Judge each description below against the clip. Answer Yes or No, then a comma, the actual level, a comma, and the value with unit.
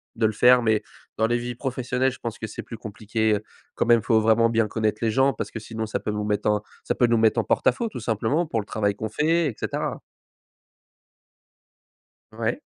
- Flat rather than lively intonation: Yes, narrow, 2.3 semitones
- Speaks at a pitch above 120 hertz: No, low, 115 Hz